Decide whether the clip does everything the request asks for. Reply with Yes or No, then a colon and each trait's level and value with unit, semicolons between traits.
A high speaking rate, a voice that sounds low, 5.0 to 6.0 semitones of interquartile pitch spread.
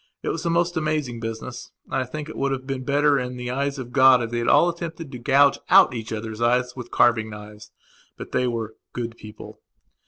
No: fast, 230 wpm; low, 125 Hz; average, 3.3 semitones